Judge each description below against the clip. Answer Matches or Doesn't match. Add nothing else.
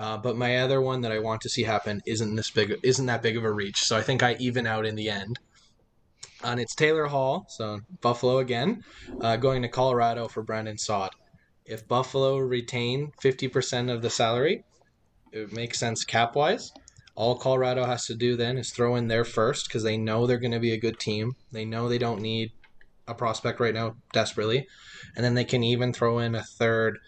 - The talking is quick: Matches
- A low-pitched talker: Matches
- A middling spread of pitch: Doesn't match